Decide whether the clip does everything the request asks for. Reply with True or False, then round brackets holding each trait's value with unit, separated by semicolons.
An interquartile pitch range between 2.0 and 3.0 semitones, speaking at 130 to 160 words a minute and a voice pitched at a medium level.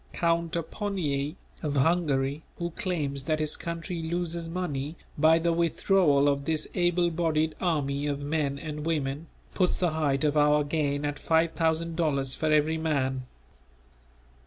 True (2.7 semitones; 150 wpm; 155 Hz)